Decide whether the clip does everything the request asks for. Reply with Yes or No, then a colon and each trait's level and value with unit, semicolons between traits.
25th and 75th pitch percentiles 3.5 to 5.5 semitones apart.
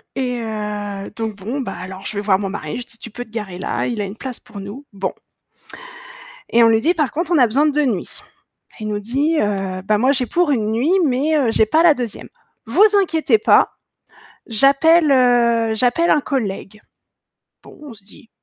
Yes: average, 5.0 semitones